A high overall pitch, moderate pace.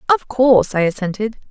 Yes: high, 220 Hz; average, 160 wpm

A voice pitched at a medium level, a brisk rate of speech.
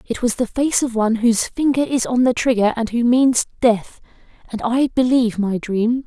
No: high, 240 Hz; fast, 210 wpm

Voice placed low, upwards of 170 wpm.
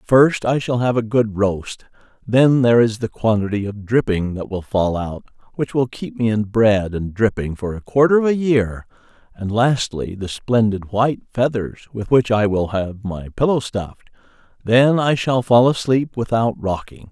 Yes: low, 115 Hz; average, 185 wpm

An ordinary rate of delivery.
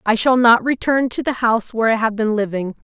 No: fast, 250 wpm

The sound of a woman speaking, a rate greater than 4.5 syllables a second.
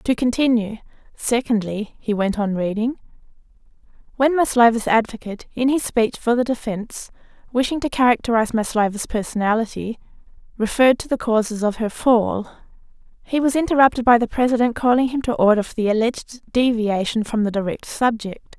Yes: female; 5.6 syllables/s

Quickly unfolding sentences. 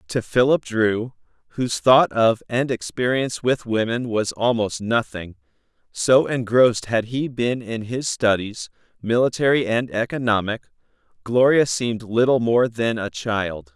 No: slow, 135 wpm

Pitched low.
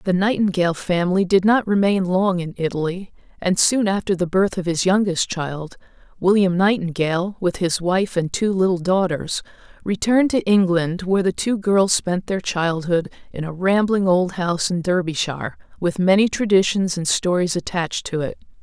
No: medium, 185 Hz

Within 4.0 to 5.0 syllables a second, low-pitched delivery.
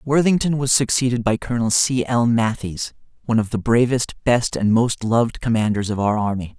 No: 5.3 syllables/s; low, 115 Hz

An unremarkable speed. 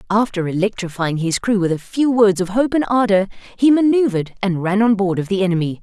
No: fast, 215 wpm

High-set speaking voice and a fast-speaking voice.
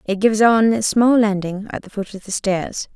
Yes: high, 210 Hz; fast, 245 wpm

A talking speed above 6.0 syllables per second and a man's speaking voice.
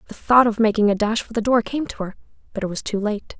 No: 6.4 syllables/s; female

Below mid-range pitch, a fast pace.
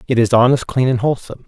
Yes: low, 120 Hz; fast, 245 wpm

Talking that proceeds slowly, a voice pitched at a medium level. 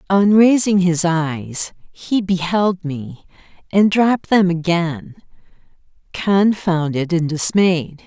Yes: slow, 105 wpm; medium, 180 Hz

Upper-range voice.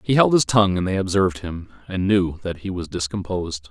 No: very low, 95 Hz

